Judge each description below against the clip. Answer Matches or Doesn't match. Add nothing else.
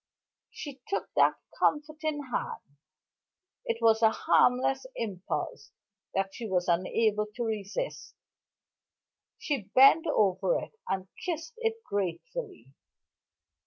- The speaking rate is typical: Doesn't match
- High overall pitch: Matches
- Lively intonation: Matches